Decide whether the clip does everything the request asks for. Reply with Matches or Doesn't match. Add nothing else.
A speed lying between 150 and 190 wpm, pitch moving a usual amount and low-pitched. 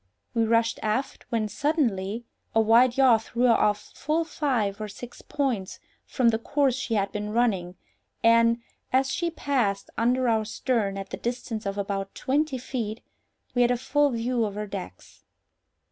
Doesn't match